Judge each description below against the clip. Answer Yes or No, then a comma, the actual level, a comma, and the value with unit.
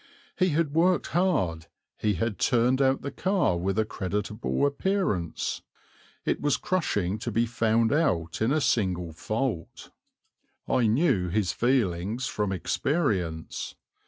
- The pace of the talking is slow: Yes, slow, 130 wpm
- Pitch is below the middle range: Yes, low, 115 Hz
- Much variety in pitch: Yes, wide, 7.3 semitones